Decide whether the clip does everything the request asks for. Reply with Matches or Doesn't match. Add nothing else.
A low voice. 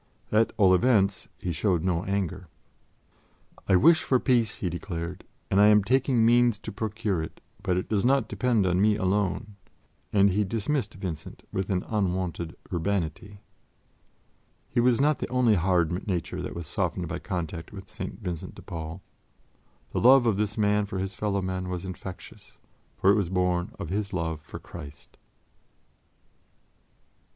Matches